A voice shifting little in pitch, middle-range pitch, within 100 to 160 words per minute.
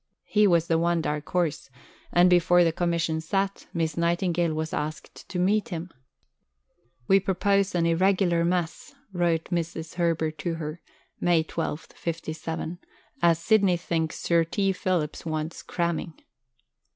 Yes: narrow, 1.7 semitones; medium, 170 Hz; average, 140 wpm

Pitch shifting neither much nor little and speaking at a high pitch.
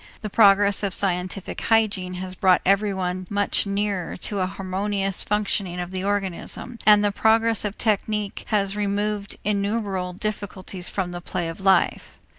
No: narrow, 1.9 semitones; high, 200 Hz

